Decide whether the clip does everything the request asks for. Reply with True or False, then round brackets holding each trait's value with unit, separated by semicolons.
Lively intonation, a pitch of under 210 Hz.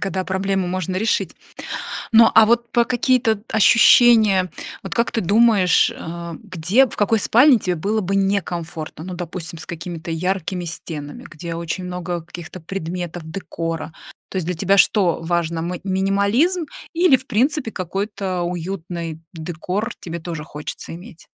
False (3.9 semitones; 185 Hz)